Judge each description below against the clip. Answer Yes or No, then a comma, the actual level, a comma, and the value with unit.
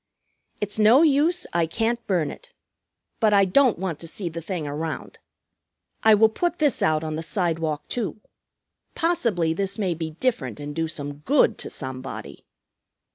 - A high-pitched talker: No, medium, 180 Hz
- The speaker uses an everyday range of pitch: No, wide, 6.1 semitones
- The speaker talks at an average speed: Yes, average, 165 wpm